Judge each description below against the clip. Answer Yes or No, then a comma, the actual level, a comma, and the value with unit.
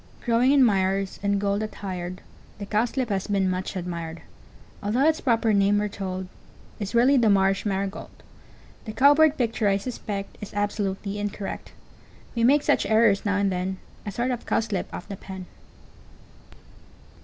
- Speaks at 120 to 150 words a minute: No, average, 165 wpm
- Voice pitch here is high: Yes, high, 205 Hz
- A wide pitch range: No, average, 3.1 semitones